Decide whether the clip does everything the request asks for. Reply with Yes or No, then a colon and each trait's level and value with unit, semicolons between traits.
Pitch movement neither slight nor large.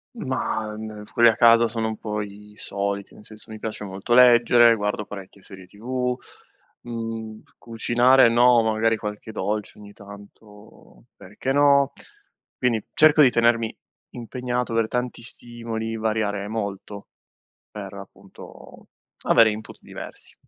No: narrow, 2.2 semitones